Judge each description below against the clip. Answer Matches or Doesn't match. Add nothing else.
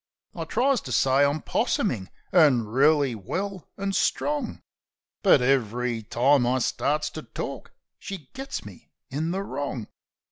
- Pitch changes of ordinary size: Doesn't match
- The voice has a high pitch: Doesn't match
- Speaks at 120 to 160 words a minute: Matches